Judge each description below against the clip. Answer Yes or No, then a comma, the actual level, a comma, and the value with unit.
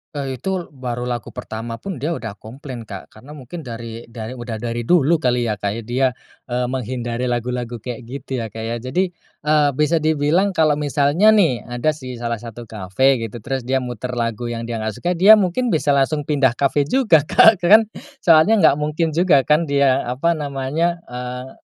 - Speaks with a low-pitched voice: Yes, low, 130 Hz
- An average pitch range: Yes, average, 4.5 semitones